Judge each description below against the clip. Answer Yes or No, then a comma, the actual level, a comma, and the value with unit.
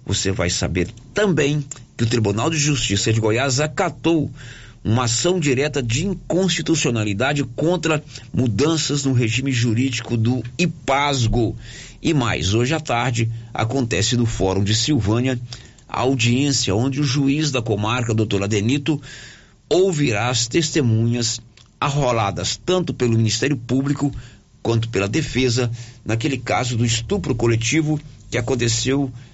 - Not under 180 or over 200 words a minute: No, average, 125 wpm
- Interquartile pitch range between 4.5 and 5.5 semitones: No, average, 3.8 semitones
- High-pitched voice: No, low, 125 Hz